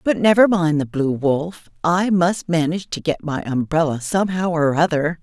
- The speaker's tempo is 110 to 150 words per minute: No, average, 185 wpm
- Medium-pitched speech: Yes, medium, 165 Hz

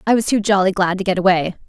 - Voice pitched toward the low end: No, high, 190 Hz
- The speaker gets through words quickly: Yes, fast, 285 wpm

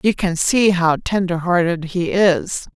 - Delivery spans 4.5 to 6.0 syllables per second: No, 3.9 syllables/s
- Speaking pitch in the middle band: Yes, medium, 180 Hz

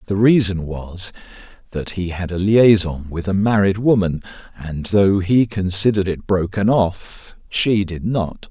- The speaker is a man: Yes, male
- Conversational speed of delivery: Yes, average, 155 wpm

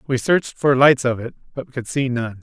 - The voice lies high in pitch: No, low, 130 Hz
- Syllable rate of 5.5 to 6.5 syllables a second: No, 5.3 syllables/s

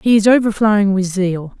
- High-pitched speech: Yes, high, 200 Hz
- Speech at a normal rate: Yes, average, 190 wpm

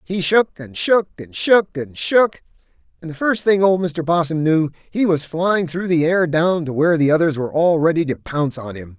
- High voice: No, medium, 165 Hz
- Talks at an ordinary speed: No, fast, 225 wpm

